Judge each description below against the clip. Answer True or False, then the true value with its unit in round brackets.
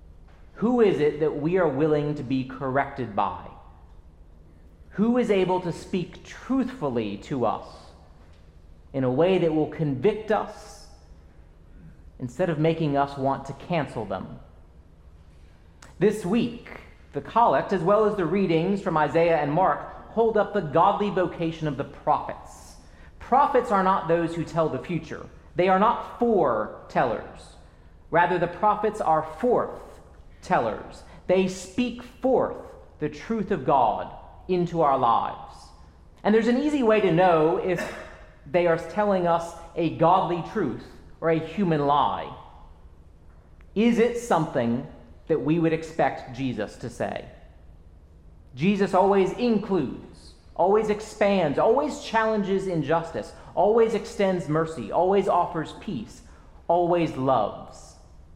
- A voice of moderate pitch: True (160 Hz)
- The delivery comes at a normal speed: False (130 wpm)